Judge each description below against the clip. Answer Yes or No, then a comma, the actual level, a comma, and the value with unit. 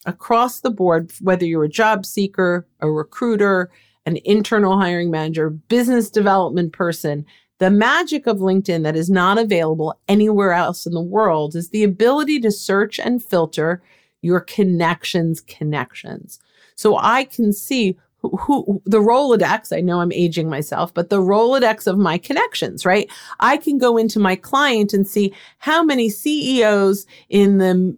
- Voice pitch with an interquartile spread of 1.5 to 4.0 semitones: No, average, 4.4 semitones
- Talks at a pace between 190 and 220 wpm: No, average, 155 wpm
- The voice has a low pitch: No, high, 195 Hz